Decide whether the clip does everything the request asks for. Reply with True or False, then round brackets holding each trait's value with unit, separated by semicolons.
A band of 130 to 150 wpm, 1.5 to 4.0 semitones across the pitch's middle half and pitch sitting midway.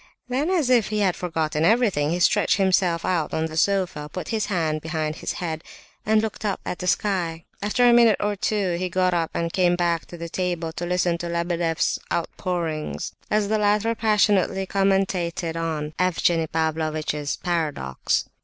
False (175 wpm; 3.6 semitones; 175 Hz)